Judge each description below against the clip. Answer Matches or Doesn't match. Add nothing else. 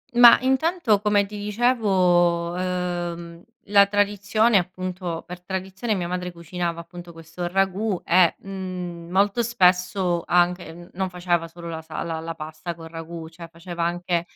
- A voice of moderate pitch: Matches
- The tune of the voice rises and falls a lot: Doesn't match